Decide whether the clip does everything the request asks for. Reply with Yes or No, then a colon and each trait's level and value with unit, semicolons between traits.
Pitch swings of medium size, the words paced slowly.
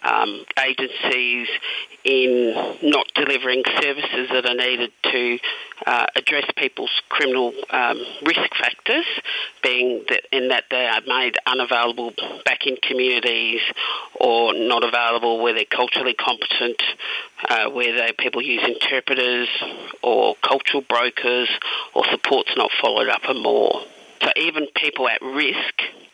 No: narrow, 1.3 semitones; slow, 130 wpm